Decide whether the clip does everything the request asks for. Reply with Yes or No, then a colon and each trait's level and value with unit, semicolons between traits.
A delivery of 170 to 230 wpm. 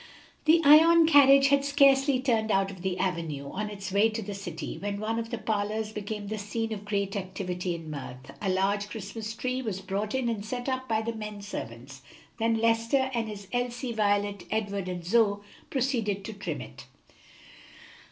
Yes: average, 185 wpm